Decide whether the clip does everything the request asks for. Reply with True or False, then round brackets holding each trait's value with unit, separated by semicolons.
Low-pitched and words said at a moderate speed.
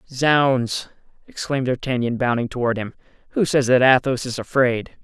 True (130 Hz; 145 wpm)